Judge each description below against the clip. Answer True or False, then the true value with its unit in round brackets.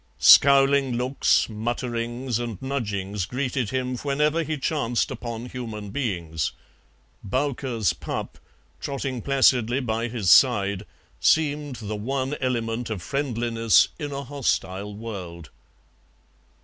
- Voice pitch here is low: True (120 Hz)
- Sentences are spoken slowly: True (110 wpm)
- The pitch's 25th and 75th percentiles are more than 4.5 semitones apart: False (4.2 semitones)